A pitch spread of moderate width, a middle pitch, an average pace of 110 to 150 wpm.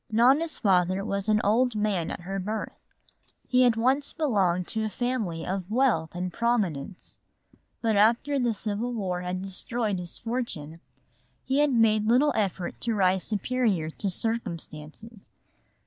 No: average, 4.6 semitones; high, 215 Hz; average, 145 wpm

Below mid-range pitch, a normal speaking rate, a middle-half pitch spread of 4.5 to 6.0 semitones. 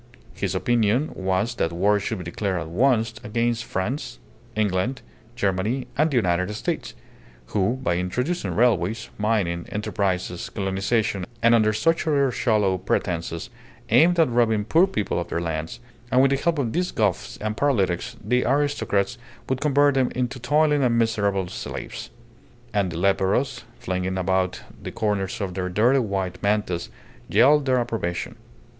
Yes: low, 110 Hz; average, 150 wpm; average, 5.2 semitones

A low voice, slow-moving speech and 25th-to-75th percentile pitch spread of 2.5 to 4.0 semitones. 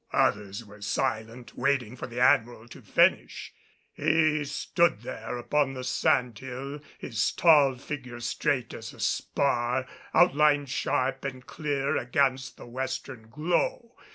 Yes: low, 130 Hz; slow, 130 wpm; average, 3.0 semitones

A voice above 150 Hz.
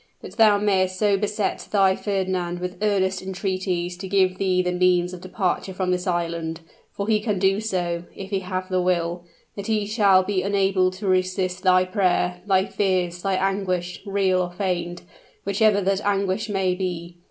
Yes: medium, 185 Hz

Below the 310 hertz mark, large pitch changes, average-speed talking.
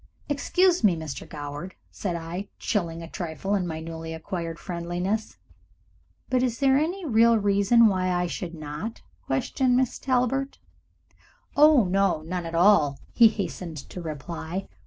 Yes: medium, 185 Hz; wide, 5.9 semitones; average, 150 wpm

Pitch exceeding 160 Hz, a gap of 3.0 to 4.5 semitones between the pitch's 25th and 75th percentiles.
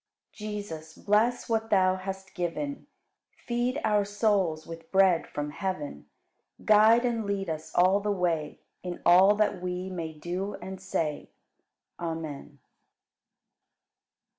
Yes: high, 190 Hz; average, 4.0 semitones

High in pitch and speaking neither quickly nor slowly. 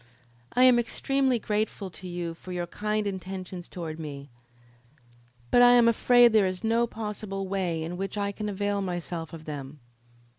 Yes: high, 195 Hz; average, 170 wpm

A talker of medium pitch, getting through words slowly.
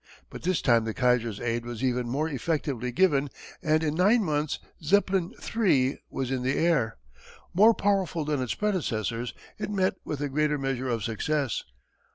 No: medium, 145 Hz; average, 170 wpm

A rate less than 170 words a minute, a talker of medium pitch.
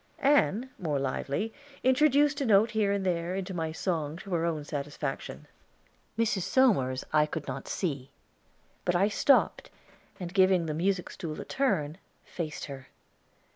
Yes: average, 150 wpm; medium, 180 Hz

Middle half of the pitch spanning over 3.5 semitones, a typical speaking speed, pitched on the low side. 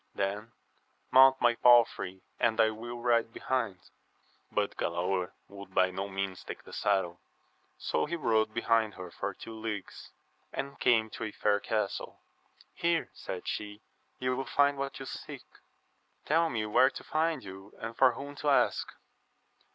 Yes: average, 4.7 semitones; average, 160 wpm; low, 110 Hz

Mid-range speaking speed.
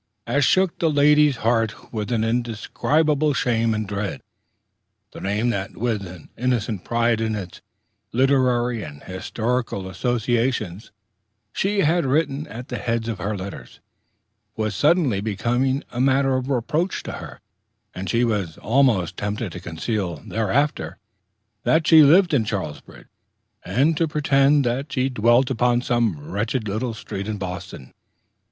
Yes: average, 145 wpm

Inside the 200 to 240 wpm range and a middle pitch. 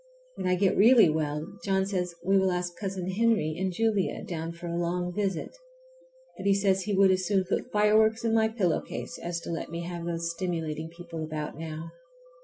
Yes: fast, 205 wpm; medium, 180 Hz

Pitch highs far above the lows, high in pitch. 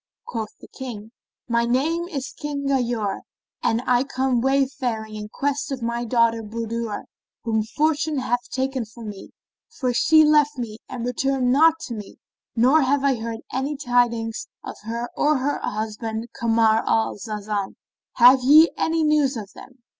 No: average, 3.5 semitones; high, 245 Hz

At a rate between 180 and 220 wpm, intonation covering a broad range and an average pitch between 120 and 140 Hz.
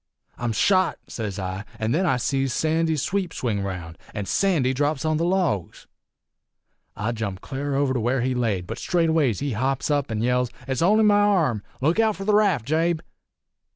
Yes: average, 190 wpm; wide, 6.6 semitones; low, 135 Hz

